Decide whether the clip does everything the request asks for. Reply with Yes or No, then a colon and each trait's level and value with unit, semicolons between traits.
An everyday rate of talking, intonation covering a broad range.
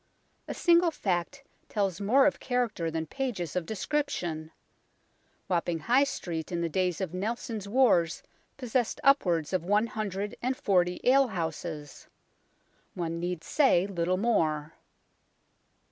No: slow, 130 wpm; wide, 6.3 semitones